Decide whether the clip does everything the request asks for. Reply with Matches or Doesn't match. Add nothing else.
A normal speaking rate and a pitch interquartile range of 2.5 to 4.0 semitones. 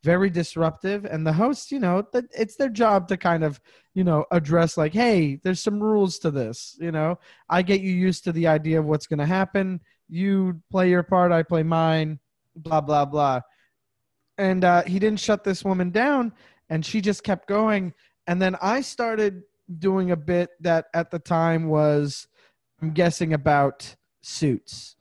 Matches